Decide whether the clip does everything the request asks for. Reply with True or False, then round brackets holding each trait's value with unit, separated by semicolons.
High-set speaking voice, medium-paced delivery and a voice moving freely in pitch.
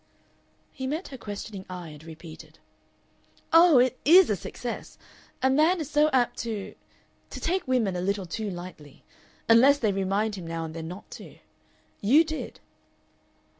True (220 Hz; 160 wpm; 7.5 semitones)